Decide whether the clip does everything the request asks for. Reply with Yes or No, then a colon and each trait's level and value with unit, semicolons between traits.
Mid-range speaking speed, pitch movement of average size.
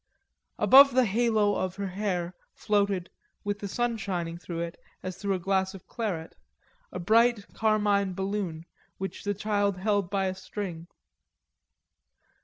No: average, 150 wpm; narrow, 2.3 semitones